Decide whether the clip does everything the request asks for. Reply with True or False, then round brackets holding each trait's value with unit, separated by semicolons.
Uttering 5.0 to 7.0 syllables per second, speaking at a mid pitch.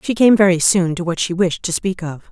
True (5.5 syllables/s; 180 Hz)